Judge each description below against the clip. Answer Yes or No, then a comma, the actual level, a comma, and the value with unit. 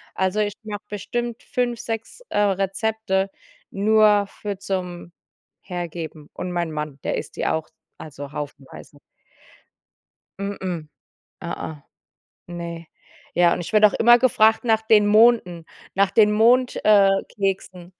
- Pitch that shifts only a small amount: No, average, 4.0 semitones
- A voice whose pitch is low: No, high, 195 Hz